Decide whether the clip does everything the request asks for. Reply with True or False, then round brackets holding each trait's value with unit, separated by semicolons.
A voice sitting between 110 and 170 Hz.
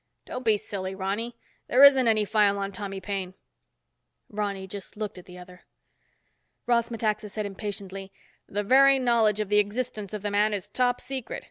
False (210 Hz)